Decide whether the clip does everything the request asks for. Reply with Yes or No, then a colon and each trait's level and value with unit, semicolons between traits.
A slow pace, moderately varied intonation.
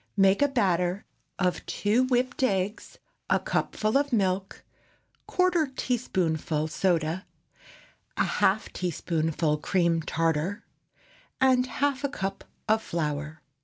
No: slow, 110 wpm; wide, 7.2 semitones